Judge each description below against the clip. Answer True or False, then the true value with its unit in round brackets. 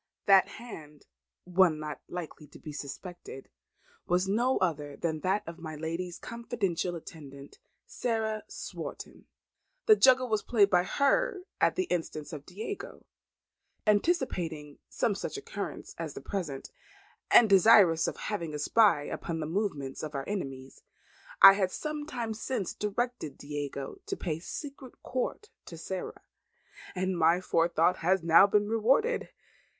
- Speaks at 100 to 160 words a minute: True (140 wpm)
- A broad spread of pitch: True (6.2 semitones)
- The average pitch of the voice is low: False (185 Hz)